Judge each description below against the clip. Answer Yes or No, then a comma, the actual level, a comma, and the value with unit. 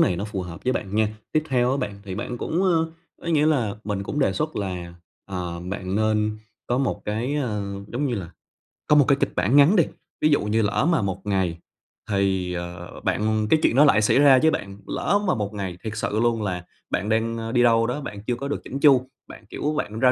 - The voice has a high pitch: No, low, 110 Hz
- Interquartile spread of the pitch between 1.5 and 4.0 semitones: No, wide, 5.6 semitones